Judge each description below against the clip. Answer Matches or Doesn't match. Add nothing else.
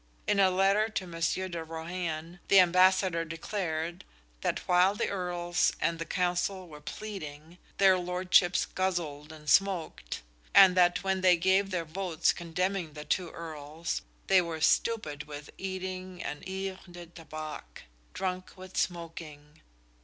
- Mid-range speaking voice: Matches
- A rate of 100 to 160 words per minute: Matches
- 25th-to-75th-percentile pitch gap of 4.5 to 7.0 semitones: Doesn't match